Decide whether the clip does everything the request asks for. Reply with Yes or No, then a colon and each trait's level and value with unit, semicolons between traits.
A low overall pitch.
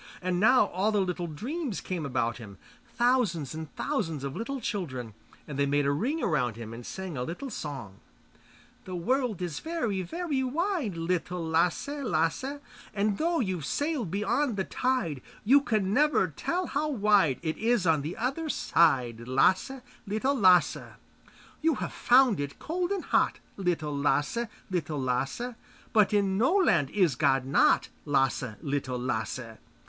No: medium, 185 Hz